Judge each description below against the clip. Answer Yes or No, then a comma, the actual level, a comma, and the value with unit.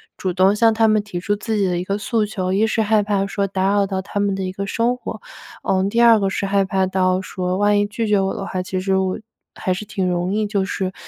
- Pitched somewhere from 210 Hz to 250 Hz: No, high, 195 Hz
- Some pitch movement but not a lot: No, narrow, 1.8 semitones